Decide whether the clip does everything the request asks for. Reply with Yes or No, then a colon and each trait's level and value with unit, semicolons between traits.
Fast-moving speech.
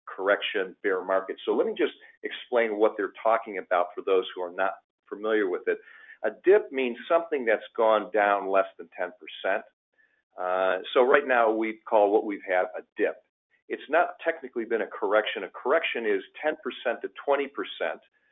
No: average, 175 wpm